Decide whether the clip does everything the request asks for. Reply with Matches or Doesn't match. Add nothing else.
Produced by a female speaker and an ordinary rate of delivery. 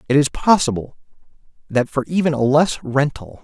Doesn't match